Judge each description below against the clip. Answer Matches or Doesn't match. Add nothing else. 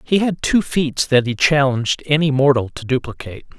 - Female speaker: Doesn't match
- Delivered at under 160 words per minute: Doesn't match